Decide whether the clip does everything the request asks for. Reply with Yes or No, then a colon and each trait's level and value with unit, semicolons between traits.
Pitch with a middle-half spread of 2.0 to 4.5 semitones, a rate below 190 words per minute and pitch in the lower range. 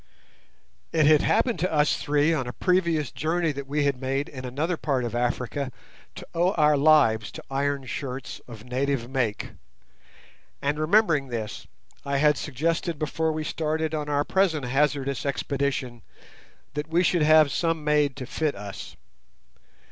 No: average, 2.8 semitones; average, 155 wpm; medium, 145 Hz